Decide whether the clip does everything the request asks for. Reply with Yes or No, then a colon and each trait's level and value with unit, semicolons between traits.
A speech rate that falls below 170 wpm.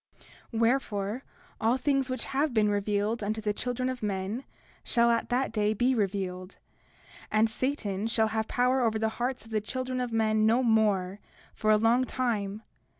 No: average, 175 wpm